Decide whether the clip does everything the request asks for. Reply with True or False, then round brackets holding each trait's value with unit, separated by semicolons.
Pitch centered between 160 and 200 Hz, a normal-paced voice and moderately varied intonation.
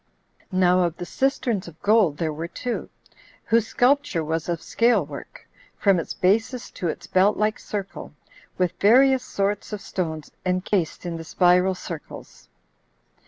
True (185 Hz; 155 wpm; 4.1 semitones)